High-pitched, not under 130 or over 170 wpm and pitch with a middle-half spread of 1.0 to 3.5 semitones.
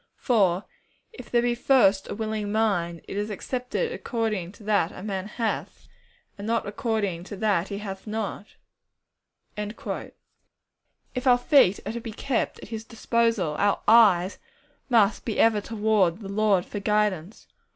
Yes: high, 210 Hz; average, 150 wpm; narrow, 2.6 semitones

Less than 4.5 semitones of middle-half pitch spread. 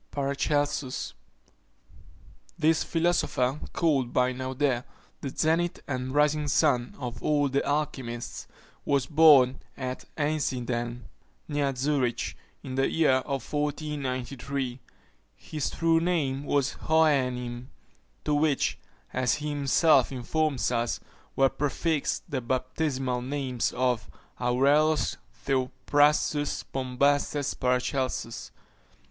Yes: average, 2.7 semitones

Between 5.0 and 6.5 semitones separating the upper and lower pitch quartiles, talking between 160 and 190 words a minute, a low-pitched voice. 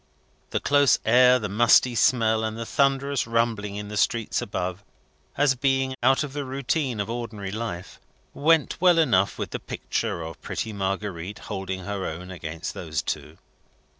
Yes: wide, 5.4 semitones; average, 165 wpm; low, 110 Hz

